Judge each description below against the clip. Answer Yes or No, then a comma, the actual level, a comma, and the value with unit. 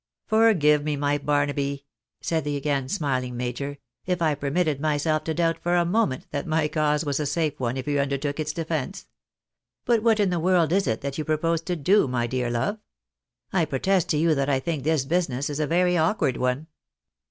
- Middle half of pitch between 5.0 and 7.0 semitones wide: No, average, 3.3 semitones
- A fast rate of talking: Yes, fast, 210 wpm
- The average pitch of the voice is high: No, medium, 150 Hz